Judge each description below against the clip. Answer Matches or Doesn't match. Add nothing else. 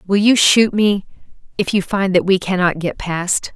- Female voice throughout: Matches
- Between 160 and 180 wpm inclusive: Doesn't match